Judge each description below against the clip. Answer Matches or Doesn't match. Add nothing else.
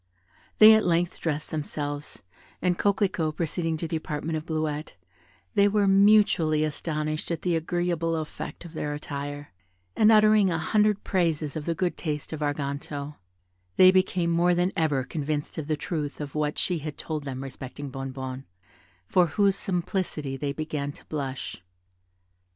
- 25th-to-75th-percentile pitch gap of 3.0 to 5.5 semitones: Matches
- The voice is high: Doesn't match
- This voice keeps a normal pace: Matches